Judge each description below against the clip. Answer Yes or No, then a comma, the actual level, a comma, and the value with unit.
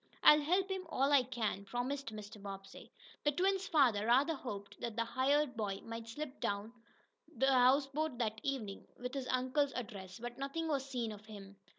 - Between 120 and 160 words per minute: No, average, 185 wpm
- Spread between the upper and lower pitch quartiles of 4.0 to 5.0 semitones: Yes, average, 4.6 semitones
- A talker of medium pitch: No, very high, 250 Hz